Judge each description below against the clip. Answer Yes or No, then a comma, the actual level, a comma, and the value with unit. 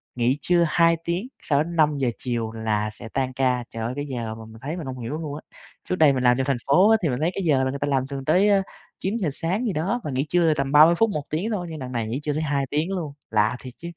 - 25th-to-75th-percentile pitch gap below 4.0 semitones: No, average, 4.8 semitones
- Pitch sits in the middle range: Yes, medium, 145 Hz